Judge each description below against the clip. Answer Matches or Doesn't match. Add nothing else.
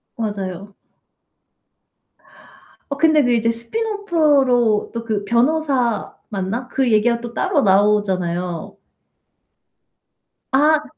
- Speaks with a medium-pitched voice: Doesn't match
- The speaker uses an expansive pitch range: Matches